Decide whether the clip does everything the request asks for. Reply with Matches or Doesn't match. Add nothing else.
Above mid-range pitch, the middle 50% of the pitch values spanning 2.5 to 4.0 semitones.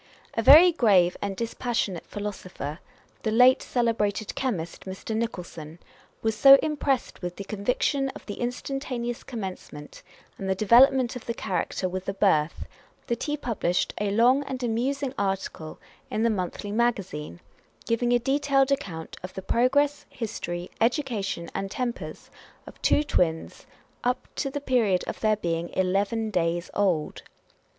Doesn't match